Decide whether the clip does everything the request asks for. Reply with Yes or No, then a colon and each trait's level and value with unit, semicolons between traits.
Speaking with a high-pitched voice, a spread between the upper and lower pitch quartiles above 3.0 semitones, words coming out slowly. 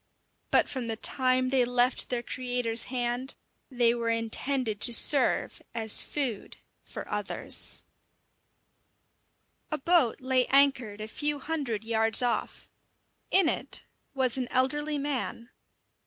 No: very high, 250 Hz; average, 2.7 semitones; slow, 125 wpm